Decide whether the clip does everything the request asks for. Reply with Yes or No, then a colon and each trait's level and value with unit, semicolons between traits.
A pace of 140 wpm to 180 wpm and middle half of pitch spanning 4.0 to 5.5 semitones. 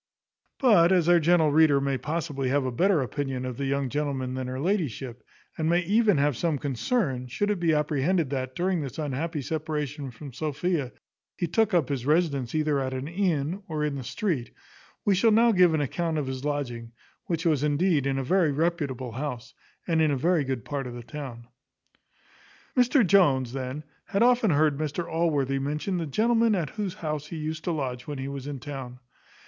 No: average, 195 wpm; average, 4.3 semitones